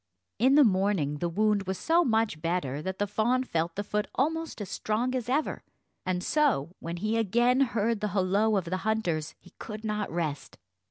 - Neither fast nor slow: Yes, average, 195 wpm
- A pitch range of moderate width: Yes, average, 4.6 semitones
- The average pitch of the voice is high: Yes, high, 210 Hz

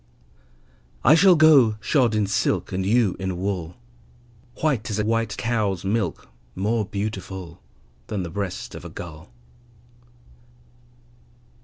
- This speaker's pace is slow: Yes, slow, 125 wpm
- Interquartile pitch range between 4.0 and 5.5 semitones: No, average, 3.3 semitones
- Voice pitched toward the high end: No, low, 105 Hz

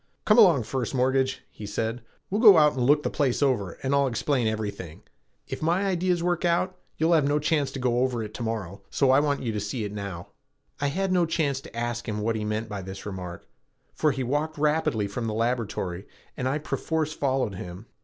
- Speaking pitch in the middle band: No, low, 130 Hz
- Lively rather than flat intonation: Yes, wide, 5.9 semitones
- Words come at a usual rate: No, fast, 220 wpm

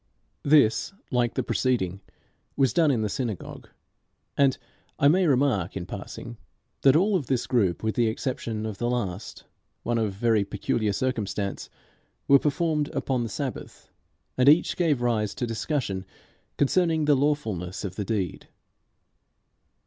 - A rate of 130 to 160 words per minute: Yes, average, 145 wpm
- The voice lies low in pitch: Yes, low, 120 Hz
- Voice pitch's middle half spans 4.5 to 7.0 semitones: Yes, average, 5.1 semitones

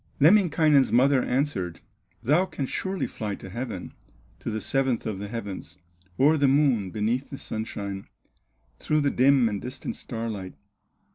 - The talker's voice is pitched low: Yes, low, 125 Hz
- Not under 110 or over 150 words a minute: Yes, average, 145 wpm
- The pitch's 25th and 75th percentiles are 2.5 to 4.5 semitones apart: No, average, 5.2 semitones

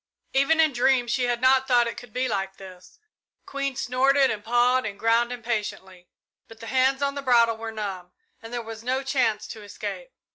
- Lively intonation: No, average, 2.9 semitones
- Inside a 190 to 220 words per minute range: Yes, average, 195 wpm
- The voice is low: No, high, 240 Hz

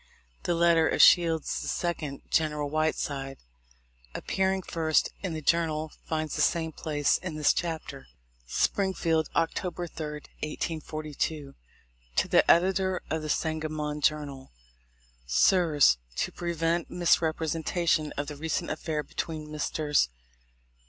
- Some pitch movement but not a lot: No, narrow, 2.0 semitones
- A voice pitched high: No, medium, 160 Hz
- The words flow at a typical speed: No, slow, 115 wpm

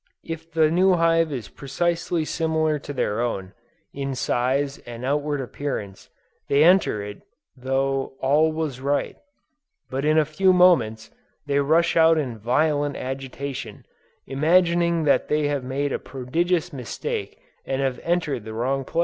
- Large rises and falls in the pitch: No, average, 3.7 semitones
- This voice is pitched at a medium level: Yes, medium, 145 Hz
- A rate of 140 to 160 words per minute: Yes, average, 150 wpm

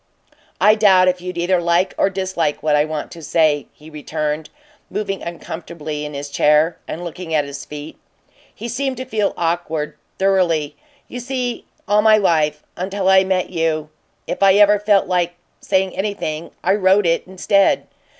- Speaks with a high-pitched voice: No, medium, 175 Hz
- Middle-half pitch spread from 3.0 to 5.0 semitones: Yes, average, 4.0 semitones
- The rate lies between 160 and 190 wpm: Yes, average, 170 wpm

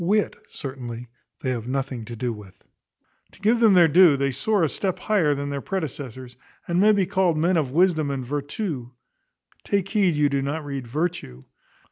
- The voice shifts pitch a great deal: Yes, wide, 5.9 semitones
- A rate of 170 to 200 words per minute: Yes, average, 185 wpm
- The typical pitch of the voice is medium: Yes, medium, 145 Hz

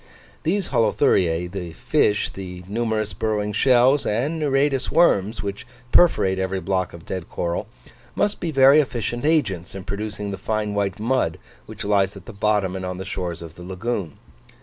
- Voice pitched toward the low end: Yes, low, 100 Hz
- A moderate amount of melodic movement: Yes, average, 4.4 semitones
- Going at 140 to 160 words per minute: No, average, 170 wpm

